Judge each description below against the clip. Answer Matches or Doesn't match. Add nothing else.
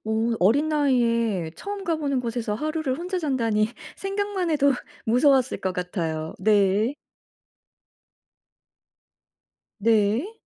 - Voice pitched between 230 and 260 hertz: Matches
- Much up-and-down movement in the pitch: Matches